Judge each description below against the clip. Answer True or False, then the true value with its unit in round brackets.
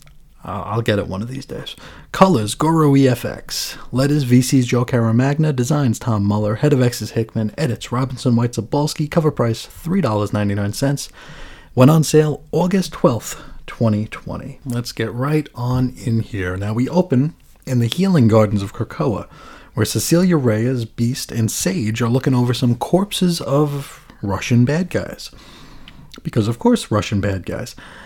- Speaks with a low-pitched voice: True (125 Hz)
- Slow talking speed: False (150 wpm)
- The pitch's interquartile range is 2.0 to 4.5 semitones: False (4.9 semitones)